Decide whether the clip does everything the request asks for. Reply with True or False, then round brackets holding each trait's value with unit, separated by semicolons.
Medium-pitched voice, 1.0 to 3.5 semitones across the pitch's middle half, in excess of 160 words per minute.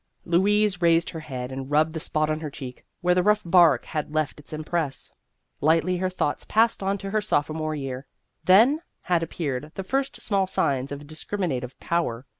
False (160 Hz; 4.3 semitones; 190 wpm)